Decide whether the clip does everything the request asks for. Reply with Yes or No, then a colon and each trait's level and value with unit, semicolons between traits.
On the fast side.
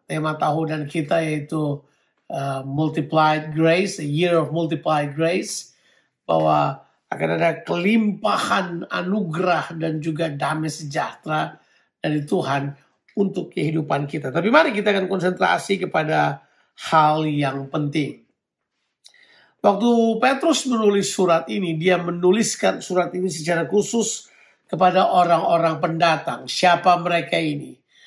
No: average, 115 wpm